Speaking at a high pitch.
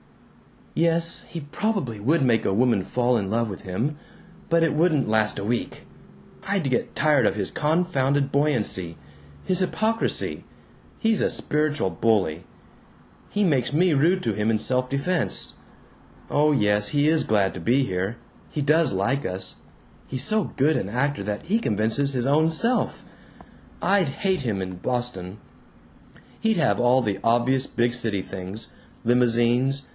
No: low, 130 Hz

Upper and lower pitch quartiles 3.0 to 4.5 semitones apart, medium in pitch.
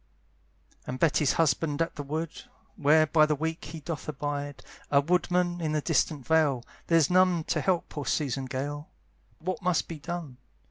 No: narrow, 2.6 semitones; medium, 155 Hz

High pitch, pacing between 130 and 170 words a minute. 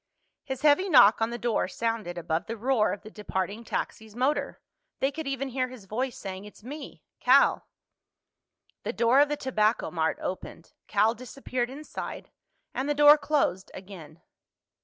Yes: high, 235 Hz; average, 160 wpm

